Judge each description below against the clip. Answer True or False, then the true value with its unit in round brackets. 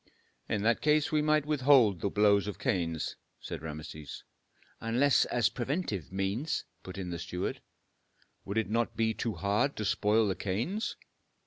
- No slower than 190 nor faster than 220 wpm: False (155 wpm)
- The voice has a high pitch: False (110 Hz)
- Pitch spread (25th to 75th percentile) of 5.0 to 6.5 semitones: True (5.6 semitones)